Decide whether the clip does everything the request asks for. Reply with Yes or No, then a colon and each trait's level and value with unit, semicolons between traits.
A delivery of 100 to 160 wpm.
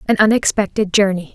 Yes: slow, 135 wpm